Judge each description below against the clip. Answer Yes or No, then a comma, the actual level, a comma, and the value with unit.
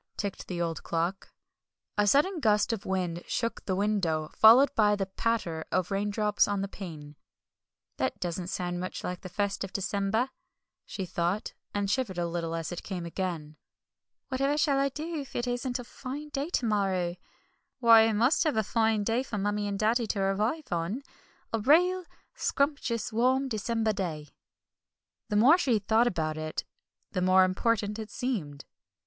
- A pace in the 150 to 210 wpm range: Yes, average, 170 wpm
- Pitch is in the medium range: No, high, 210 Hz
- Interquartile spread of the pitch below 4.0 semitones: No, average, 4.8 semitones